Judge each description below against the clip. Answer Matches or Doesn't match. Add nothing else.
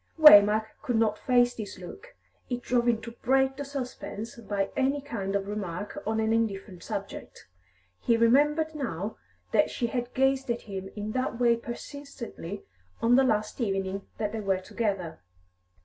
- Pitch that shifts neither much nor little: Matches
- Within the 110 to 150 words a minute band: Doesn't match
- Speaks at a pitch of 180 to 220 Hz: Doesn't match